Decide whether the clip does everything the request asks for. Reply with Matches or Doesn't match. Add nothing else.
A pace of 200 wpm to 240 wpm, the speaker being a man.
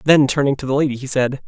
Doesn't match